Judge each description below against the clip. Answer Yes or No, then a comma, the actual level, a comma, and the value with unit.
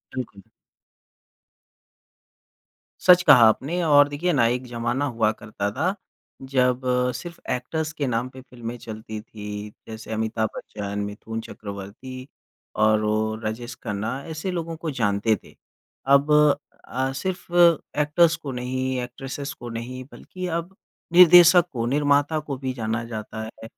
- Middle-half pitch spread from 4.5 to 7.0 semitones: Yes, average, 4.9 semitones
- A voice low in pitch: Yes, low, 125 Hz